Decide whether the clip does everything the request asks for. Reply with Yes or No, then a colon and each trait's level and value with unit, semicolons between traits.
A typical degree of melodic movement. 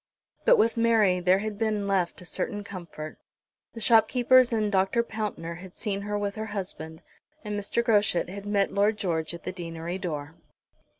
Yes: average, 3.3 semitones